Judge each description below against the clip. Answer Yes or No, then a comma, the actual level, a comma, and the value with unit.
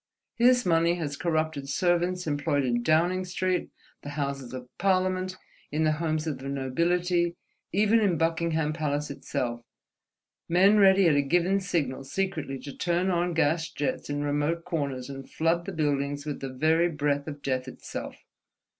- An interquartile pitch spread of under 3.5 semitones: No, average, 3.8 semitones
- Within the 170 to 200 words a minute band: No, average, 160 wpm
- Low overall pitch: No, medium, 160 Hz